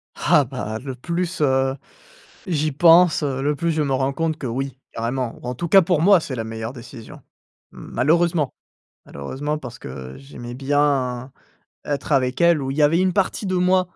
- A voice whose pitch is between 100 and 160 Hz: Yes, medium, 140 Hz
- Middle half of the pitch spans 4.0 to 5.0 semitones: Yes, average, 4.5 semitones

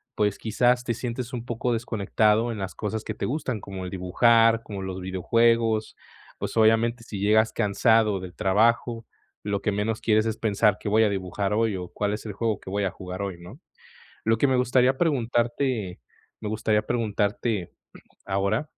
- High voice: No, low, 110 Hz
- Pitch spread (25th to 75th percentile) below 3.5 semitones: Yes, average, 2.8 semitones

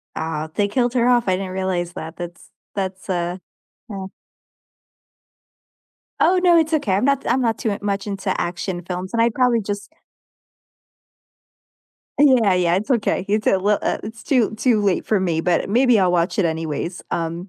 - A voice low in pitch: No, high, 195 Hz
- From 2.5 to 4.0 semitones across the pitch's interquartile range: No, average, 4.5 semitones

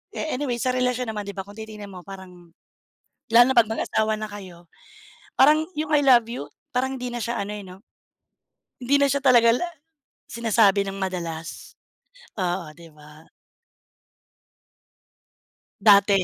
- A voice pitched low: No, high, 215 Hz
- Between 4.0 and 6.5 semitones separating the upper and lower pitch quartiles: Yes, average, 4.7 semitones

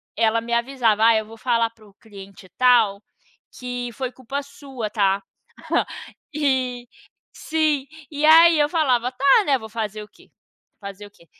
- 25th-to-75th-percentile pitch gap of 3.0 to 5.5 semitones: Yes, average, 3.9 semitones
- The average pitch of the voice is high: Yes, high, 240 Hz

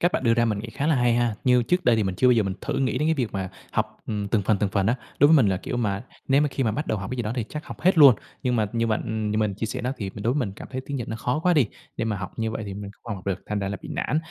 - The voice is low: Yes, low, 115 Hz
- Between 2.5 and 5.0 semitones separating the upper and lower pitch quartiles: Yes, average, 3.8 semitones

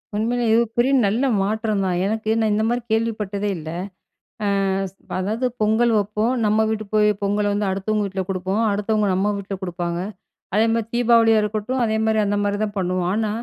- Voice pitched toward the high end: Yes, high, 210 Hz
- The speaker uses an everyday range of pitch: No, narrow, 1.9 semitones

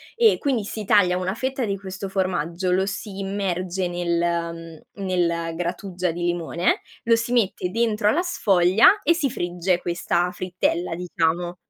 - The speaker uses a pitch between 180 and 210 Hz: Yes, medium, 185 Hz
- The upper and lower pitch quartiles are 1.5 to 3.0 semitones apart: Yes, average, 2.7 semitones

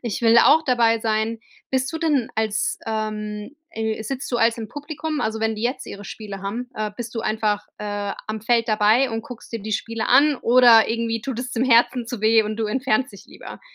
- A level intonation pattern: Yes, narrow, 2.3 semitones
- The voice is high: Yes, high, 225 Hz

